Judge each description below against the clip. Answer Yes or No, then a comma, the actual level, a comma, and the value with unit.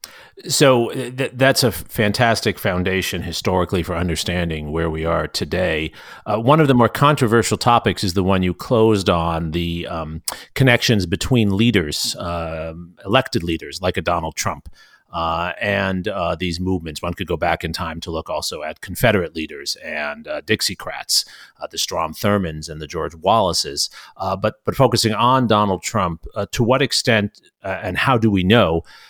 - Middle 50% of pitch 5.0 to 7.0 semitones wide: Yes, wide, 5.5 semitones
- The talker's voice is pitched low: Yes, very low, 95 Hz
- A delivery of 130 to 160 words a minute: No, average, 170 wpm